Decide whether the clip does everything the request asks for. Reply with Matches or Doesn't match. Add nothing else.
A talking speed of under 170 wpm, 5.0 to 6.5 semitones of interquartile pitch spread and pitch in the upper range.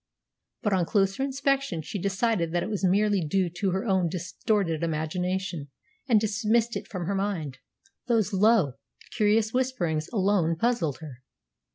Doesn't match